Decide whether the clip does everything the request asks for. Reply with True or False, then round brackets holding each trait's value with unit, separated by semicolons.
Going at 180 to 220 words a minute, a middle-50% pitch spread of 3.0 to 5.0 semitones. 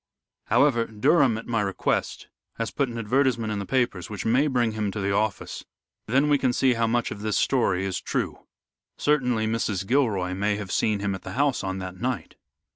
True (200 wpm; 4.0 semitones)